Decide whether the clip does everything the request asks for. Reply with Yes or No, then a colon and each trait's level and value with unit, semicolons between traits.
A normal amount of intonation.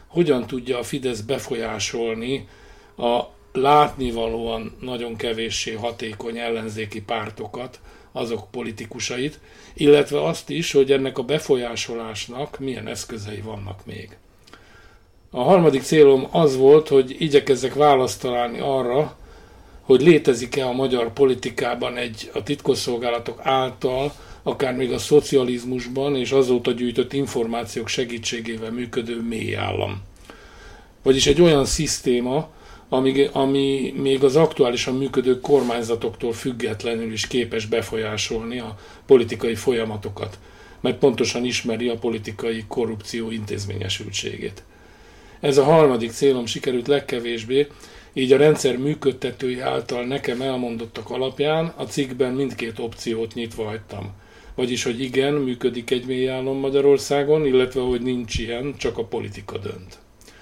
Yes: average, 3.1 semitones